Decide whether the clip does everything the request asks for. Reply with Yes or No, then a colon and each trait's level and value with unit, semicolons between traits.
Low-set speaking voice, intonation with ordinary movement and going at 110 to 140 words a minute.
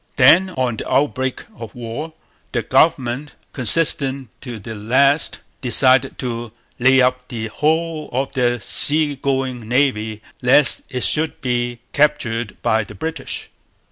Yes: low, 130 Hz; average, 3.2 semitones; slow, 135 wpm